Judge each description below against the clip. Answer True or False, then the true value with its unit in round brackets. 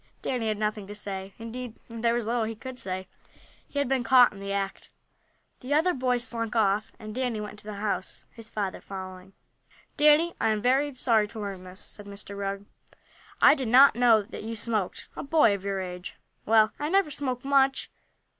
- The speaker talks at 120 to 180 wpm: False (200 wpm)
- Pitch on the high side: True (220 Hz)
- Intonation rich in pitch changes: False (4.0 semitones)